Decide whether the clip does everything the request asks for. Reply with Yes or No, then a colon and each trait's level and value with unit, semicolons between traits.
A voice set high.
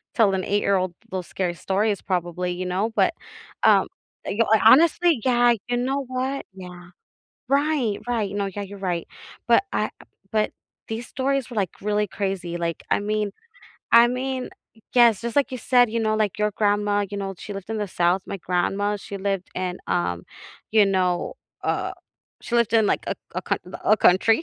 Yes: high, 205 Hz